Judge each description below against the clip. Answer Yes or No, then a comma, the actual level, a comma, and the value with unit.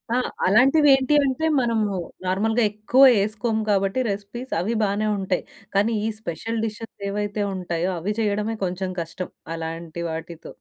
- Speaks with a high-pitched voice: Yes, high, 205 Hz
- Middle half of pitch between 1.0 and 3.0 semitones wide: No, average, 3.5 semitones